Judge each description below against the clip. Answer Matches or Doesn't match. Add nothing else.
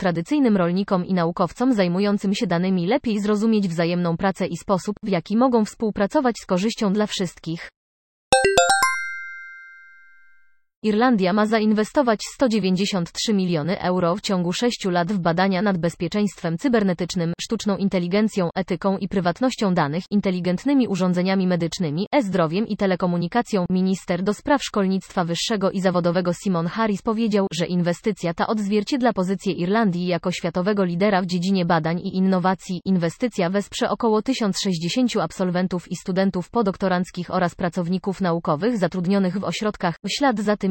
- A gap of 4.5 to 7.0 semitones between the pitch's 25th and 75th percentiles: Doesn't match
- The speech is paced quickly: Doesn't match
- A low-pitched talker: Doesn't match